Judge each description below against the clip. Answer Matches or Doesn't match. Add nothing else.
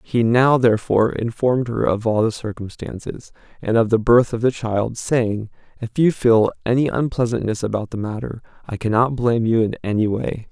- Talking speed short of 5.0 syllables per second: Doesn't match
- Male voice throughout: Matches